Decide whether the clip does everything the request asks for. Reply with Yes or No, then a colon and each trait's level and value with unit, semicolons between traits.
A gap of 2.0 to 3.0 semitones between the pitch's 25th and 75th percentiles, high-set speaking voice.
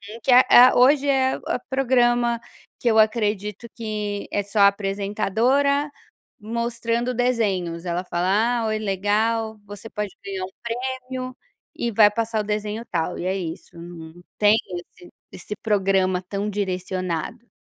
No: average, 3.6 semitones; high, 210 Hz